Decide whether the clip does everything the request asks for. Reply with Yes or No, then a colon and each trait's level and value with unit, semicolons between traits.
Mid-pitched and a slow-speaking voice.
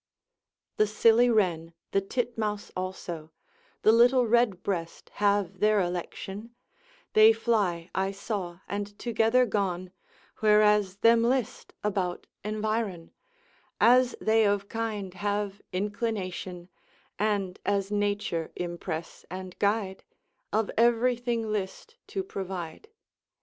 No: high, 205 Hz; slow, 105 wpm